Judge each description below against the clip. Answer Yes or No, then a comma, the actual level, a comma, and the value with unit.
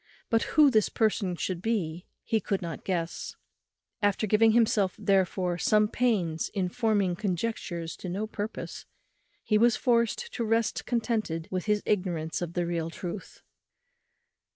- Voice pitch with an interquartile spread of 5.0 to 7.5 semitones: No, average, 4.2 semitones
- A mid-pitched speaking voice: No, high, 205 Hz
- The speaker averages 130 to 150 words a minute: Yes, average, 145 wpm